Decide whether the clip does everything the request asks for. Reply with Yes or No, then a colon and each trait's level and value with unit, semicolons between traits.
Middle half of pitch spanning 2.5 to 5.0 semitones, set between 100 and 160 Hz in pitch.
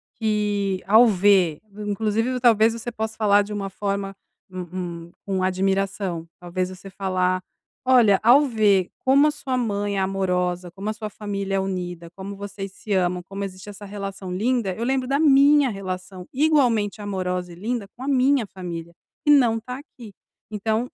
No: average, 3.4 semitones; high, 200 Hz